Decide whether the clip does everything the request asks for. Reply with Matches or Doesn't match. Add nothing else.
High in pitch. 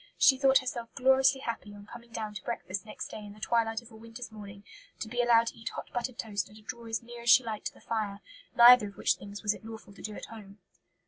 Matches